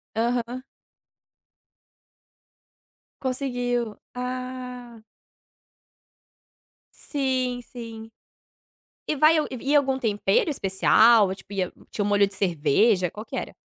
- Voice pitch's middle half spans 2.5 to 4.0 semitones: Yes, average, 3.6 semitones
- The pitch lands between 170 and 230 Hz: No, high, 240 Hz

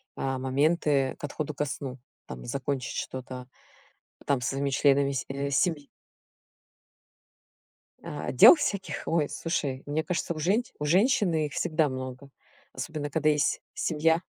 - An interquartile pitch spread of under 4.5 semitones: Yes, average, 3.0 semitones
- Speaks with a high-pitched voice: No, medium, 145 Hz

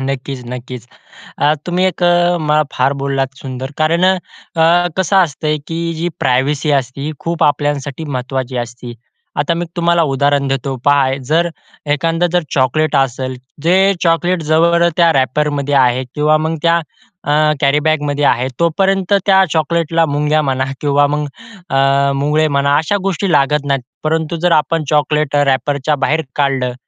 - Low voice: No, medium, 150 Hz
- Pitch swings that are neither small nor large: Yes, average, 3.3 semitones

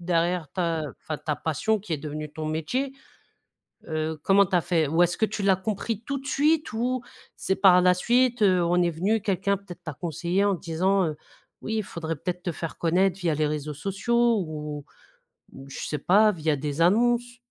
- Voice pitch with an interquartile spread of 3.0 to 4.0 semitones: No, average, 4.7 semitones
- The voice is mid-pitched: Yes, medium, 180 Hz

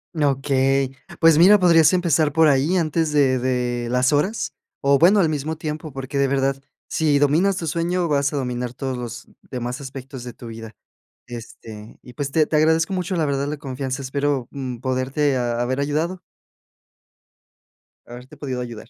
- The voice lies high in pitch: No, medium, 140 Hz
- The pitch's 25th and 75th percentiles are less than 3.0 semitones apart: No, average, 3.5 semitones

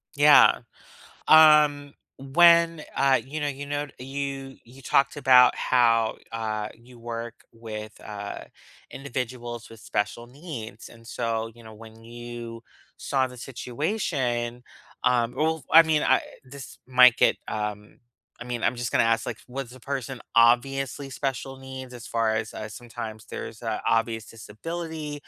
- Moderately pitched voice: No, low, 125 Hz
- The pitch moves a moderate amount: Yes, average, 3.2 semitones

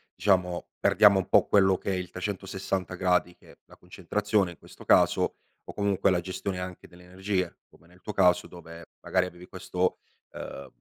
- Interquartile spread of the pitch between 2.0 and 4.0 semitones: No, narrow, 1.4 semitones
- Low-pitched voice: Yes, very low, 90 Hz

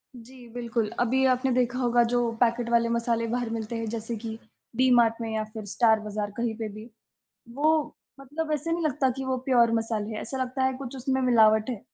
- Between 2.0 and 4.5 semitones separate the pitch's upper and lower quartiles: Yes, narrow, 2.4 semitones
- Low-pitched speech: No, high, 235 Hz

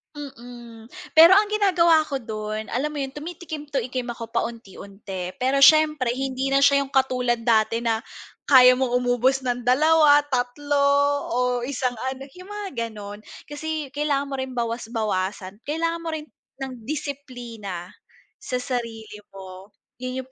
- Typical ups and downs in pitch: Yes, average, 4.1 semitones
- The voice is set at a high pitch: Yes, very high, 255 Hz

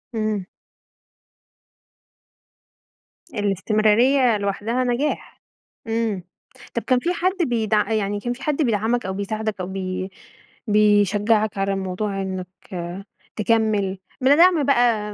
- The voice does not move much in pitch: No, average, 3.3 semitones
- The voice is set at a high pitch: Yes, high, 215 Hz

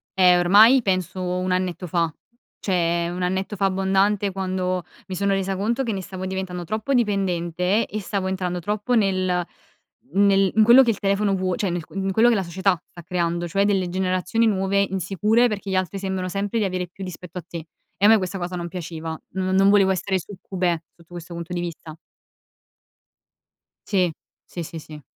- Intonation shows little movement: Yes, narrow, 1.9 semitones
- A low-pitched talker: No, medium, 185 Hz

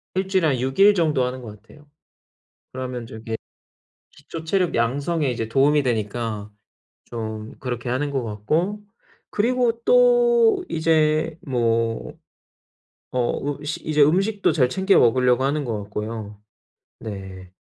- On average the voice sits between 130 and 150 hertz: Yes, low, 135 Hz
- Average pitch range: No, wide, 6.3 semitones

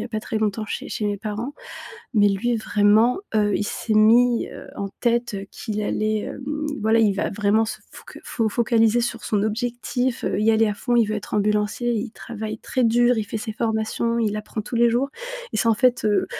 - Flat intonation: Yes, narrow, 2.1 semitones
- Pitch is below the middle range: No, high, 220 Hz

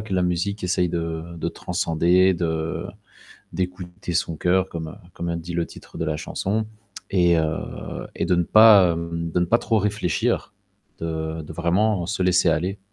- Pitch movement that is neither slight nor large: No, narrow, 2.1 semitones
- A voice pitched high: No, very low, 85 Hz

